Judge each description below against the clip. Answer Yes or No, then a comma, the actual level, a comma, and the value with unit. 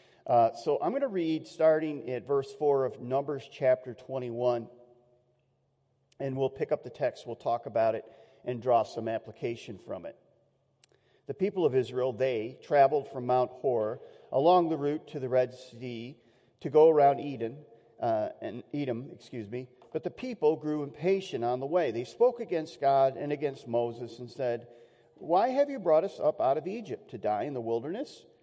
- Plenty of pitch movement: No, average, 3.8 semitones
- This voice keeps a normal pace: Yes, average, 180 wpm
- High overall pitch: No, low, 135 Hz